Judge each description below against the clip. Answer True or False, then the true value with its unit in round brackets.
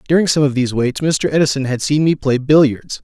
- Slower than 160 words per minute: False (235 wpm)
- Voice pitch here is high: False (140 Hz)